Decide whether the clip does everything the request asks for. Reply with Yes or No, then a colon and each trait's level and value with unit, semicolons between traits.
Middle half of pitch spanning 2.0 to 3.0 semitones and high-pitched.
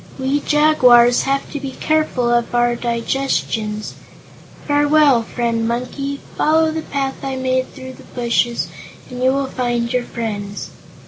Yes: average, 2.7 semitones; very high, 255 Hz